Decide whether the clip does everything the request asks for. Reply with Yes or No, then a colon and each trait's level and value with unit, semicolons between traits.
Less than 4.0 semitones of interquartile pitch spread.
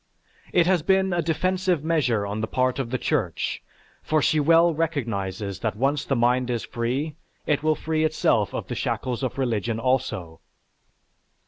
No: average, 5.3 semitones